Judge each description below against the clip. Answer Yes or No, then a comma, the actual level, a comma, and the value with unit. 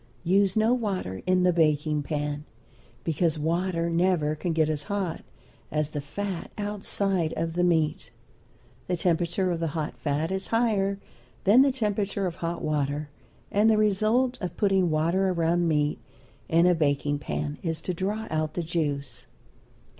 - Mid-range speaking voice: Yes, medium, 170 Hz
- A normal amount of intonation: Yes, average, 4.0 semitones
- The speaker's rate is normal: Yes, average, 160 wpm